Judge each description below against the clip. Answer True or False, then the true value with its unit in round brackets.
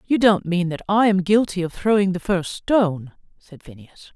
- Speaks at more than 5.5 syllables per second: False (4.9 syllables/s)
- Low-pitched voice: False (195 Hz)